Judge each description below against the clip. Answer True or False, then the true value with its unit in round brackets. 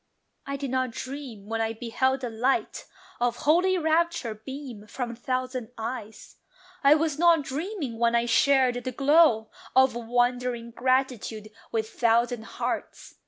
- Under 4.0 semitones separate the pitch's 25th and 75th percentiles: True (3.2 semitones)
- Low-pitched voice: False (250 Hz)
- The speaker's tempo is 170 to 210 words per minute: False (140 wpm)